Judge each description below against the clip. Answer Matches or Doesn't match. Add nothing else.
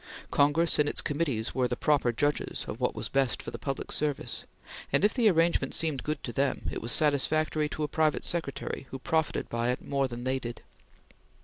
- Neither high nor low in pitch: Matches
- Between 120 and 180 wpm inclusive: Doesn't match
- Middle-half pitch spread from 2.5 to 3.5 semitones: Matches